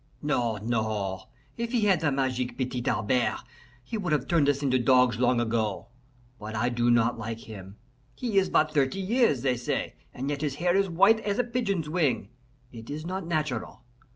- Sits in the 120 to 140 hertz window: Yes, low, 135 Hz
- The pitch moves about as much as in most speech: No, wide, 6.6 semitones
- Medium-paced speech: Yes, average, 190 wpm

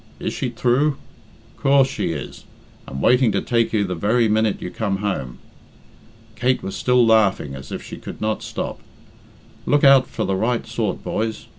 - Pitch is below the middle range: Yes, low, 110 Hz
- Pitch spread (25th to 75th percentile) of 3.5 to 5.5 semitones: Yes, average, 4.3 semitones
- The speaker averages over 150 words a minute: Yes, average, 175 wpm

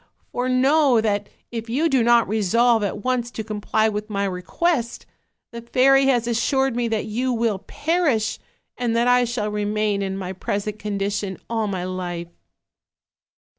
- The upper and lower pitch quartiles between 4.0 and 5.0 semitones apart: No, average, 3.2 semitones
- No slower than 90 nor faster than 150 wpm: No, average, 165 wpm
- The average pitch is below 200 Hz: No, high, 225 Hz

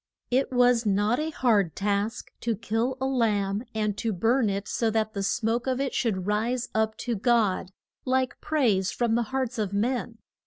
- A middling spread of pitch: Yes, average, 3.2 semitones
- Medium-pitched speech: No, high, 225 Hz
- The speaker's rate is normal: Yes, average, 185 wpm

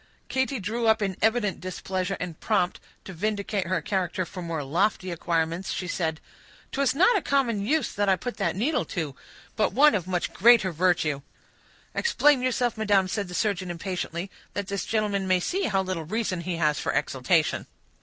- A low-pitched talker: No, high, 190 Hz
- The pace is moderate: Yes, average, 175 wpm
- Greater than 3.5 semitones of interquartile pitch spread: Yes, average, 4.1 semitones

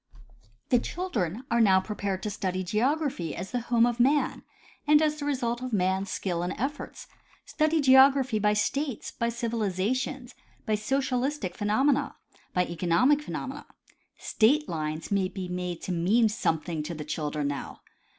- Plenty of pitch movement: Yes, wide, 6.4 semitones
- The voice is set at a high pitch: Yes, high, 215 Hz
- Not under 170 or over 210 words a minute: No, average, 155 wpm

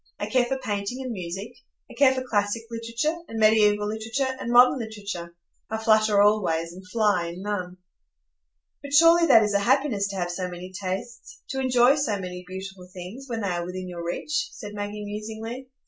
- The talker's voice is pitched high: Yes, high, 210 Hz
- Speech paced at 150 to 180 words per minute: No, average, 190 wpm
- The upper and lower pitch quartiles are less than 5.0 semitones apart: Yes, average, 4.6 semitones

